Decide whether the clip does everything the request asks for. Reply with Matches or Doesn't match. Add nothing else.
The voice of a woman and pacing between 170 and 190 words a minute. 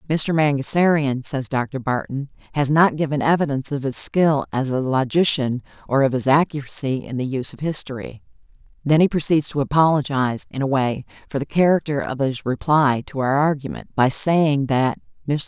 Matches